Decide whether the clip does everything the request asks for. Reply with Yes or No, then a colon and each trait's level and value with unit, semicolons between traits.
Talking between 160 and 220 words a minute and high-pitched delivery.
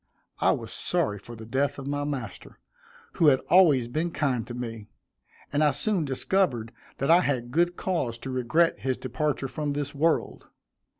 No: average, 175 wpm; medium, 140 Hz